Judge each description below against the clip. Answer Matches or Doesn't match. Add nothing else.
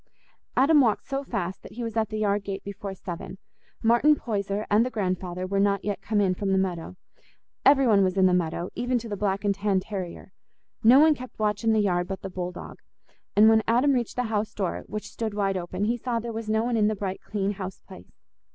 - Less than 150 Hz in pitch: Doesn't match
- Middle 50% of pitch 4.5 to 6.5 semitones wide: Doesn't match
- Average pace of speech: Doesn't match